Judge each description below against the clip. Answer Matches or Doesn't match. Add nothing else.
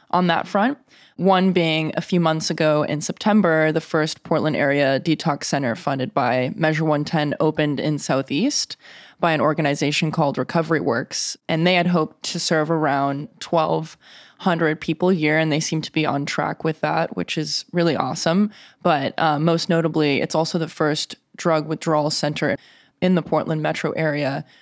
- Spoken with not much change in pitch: Matches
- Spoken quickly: Doesn't match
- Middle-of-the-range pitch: Matches